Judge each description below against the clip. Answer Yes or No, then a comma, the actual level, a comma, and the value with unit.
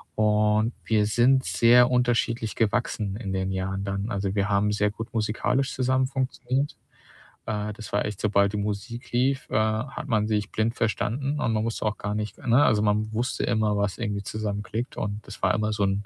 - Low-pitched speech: Yes, low, 110 Hz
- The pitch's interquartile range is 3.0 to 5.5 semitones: No, narrow, 2.5 semitones